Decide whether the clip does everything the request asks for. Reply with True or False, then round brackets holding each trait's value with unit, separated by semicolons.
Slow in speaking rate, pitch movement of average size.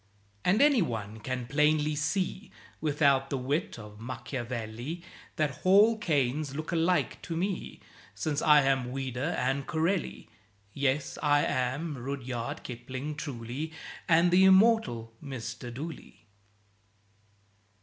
True (115 wpm; 4.5 semitones)